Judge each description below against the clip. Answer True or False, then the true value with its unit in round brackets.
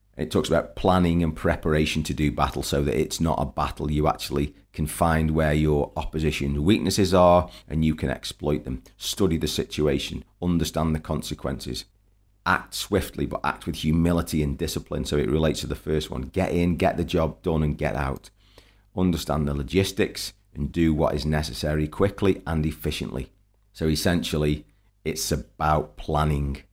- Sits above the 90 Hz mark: False (80 Hz)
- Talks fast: False (170 wpm)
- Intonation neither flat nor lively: True (3.4 semitones)